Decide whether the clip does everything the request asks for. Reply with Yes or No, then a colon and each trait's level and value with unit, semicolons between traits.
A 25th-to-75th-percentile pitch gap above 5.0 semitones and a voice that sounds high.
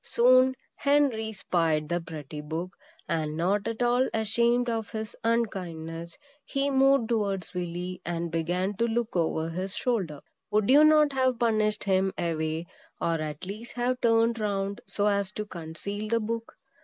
Yes: wide, 5.6 semitones; high, 205 Hz